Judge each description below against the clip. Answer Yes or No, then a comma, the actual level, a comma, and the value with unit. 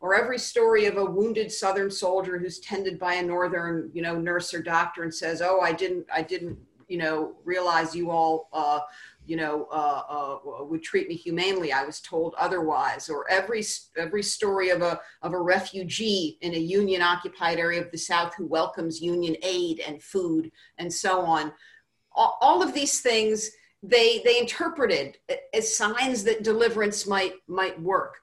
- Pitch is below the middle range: No, medium, 185 Hz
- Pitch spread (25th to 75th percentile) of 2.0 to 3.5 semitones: No, average, 4.4 semitones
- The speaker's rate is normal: Yes, average, 180 wpm